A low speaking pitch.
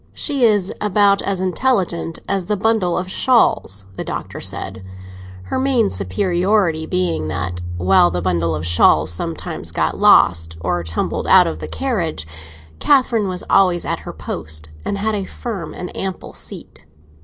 No: medium, 175 Hz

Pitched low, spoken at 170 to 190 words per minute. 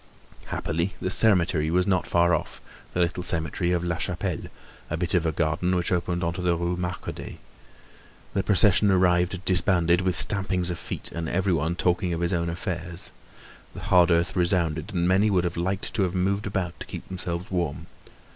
Yes: very low, 90 Hz; average, 185 wpm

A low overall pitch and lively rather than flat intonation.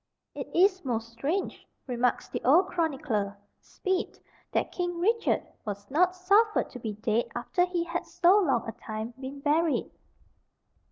No: very high, 300 Hz; wide, 7.6 semitones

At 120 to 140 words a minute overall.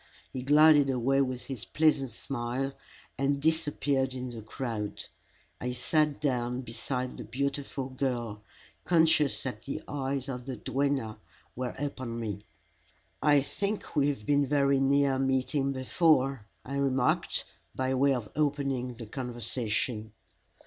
Yes: slow, 135 wpm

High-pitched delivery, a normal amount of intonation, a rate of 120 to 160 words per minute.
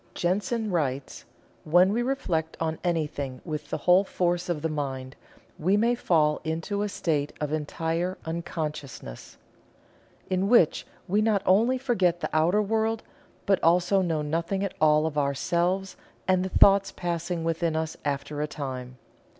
No: medium, 170 Hz; average, 4.1 semitones; average, 150 wpm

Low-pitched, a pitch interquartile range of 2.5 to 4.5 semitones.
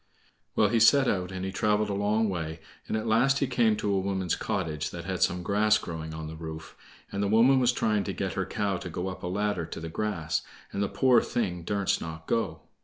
Yes: low, 100 Hz; average, 4.1 semitones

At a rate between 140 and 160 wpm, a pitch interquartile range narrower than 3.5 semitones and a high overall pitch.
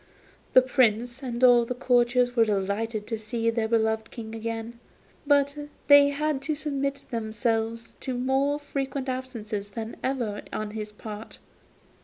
Yes: average, 145 wpm; average, 3.1 semitones; high, 235 Hz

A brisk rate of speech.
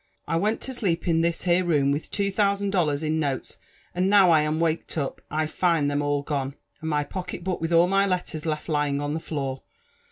Yes: fast, 220 wpm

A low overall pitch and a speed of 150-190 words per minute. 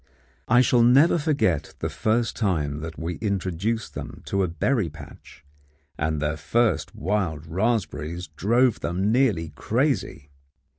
No: very low, 95 Hz; slow, 135 wpm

